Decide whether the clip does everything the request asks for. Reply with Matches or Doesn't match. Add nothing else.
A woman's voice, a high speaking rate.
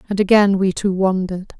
Doesn't match